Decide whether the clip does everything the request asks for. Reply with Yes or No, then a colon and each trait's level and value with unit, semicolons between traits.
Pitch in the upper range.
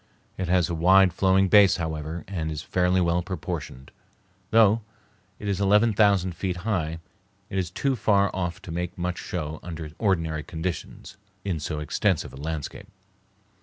No: very low, 90 Hz